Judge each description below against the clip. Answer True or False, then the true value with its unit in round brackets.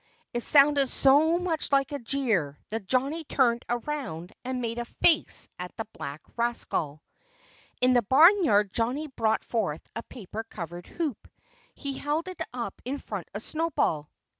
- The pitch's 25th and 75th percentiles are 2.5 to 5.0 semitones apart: False (5.5 semitones)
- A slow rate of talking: False (155 wpm)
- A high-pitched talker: True (245 Hz)